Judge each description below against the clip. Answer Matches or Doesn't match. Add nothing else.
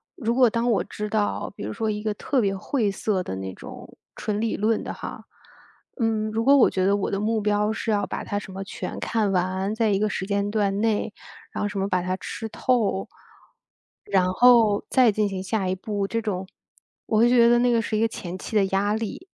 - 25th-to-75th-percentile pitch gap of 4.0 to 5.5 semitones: Doesn't match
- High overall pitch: Matches